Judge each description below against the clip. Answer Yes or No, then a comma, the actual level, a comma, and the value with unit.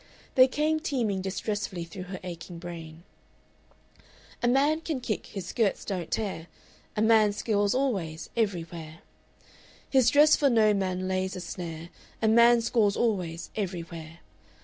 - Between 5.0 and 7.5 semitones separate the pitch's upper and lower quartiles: Yes, average, 5.3 semitones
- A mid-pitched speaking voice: No, high, 200 Hz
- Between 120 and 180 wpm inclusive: Yes, average, 140 wpm